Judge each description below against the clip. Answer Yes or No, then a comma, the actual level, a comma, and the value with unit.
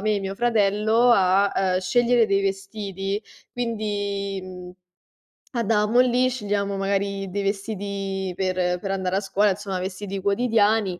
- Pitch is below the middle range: No, high, 200 Hz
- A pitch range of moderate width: No, narrow, 1.8 semitones